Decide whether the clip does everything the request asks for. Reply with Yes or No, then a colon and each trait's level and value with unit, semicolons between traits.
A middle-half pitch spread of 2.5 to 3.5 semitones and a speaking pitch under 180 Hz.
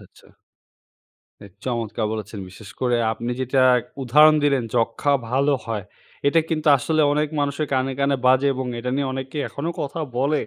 Yes: average, 3.2 semitones; low, 135 Hz